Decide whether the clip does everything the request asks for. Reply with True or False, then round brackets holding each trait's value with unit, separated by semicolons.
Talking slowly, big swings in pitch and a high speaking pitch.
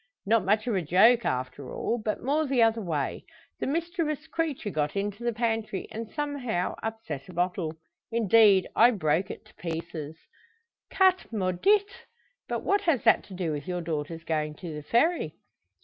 False (165 wpm; 6.8 semitones; 210 Hz)